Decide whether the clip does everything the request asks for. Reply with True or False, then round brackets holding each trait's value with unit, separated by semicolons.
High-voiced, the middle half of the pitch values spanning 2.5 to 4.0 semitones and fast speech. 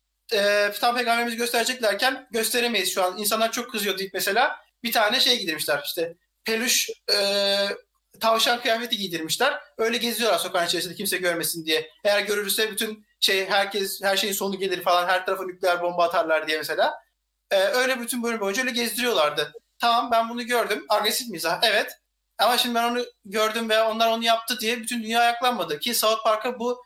True (220 Hz; 3.5 semitones; 175 wpm)